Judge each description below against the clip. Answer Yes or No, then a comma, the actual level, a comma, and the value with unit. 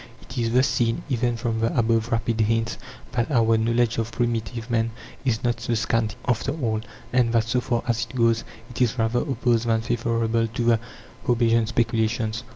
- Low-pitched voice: Yes, low, 115 Hz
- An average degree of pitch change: No, narrow, 1.0 semitones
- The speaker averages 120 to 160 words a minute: No, average, 185 wpm